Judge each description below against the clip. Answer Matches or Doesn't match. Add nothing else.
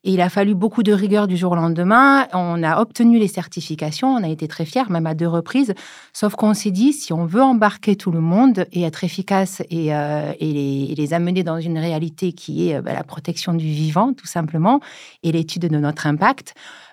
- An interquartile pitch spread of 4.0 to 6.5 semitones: Matches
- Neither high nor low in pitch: Matches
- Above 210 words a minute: Matches